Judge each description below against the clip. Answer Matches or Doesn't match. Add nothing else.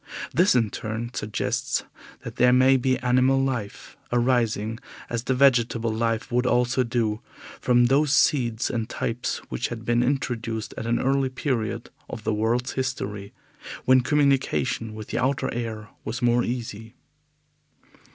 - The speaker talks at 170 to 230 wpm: Doesn't match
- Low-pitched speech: Matches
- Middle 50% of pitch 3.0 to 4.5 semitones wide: Doesn't match